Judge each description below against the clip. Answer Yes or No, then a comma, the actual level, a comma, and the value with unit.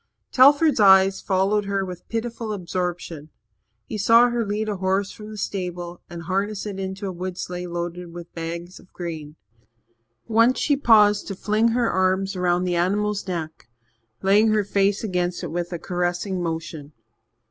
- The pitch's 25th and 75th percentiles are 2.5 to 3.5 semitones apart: Yes, average, 3.0 semitones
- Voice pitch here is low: No, high, 190 Hz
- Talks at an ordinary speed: Yes, average, 165 wpm